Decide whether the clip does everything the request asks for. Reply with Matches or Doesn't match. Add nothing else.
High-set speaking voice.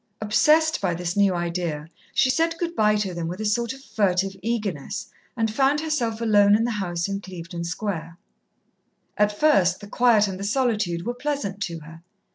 Matches